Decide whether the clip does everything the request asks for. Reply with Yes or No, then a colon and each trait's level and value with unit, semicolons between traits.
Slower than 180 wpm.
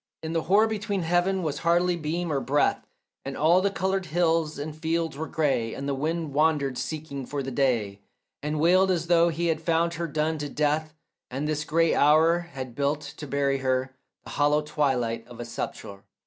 No: average, 190 wpm